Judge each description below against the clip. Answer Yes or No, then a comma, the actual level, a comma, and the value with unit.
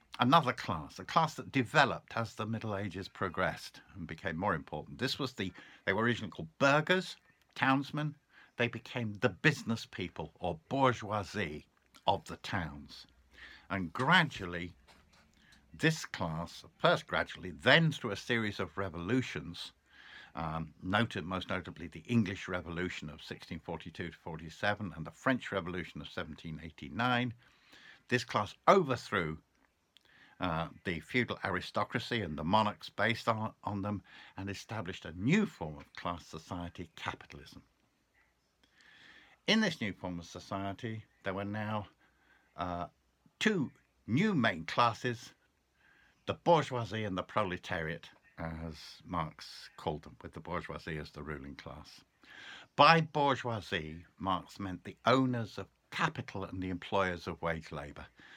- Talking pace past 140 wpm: No, slow, 135 wpm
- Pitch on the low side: Yes, low, 100 Hz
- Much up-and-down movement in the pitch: Yes, wide, 6.0 semitones